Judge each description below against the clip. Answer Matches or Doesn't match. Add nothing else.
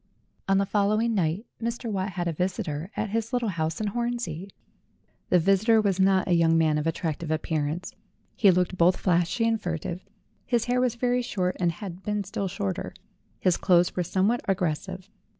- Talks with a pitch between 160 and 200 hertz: Matches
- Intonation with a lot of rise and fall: Doesn't match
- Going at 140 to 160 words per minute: Doesn't match